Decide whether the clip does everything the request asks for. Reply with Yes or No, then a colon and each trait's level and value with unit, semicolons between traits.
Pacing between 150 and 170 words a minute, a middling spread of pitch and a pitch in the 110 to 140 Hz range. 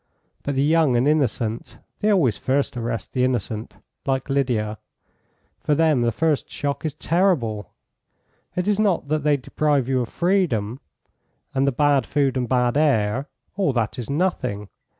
Yes: average, 160 wpm; average, 4.3 semitones; low, 135 Hz